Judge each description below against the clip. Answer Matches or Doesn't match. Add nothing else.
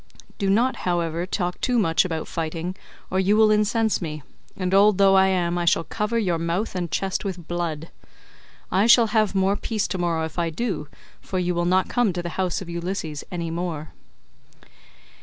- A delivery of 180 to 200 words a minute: Matches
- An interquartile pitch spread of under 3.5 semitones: Matches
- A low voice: Doesn't match